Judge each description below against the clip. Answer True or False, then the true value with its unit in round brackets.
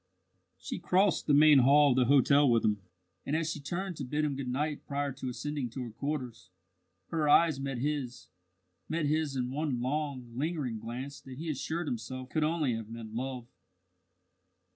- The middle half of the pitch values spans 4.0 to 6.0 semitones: False (3.4 semitones)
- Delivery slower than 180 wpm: False (185 wpm)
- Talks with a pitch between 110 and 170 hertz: True (140 Hz)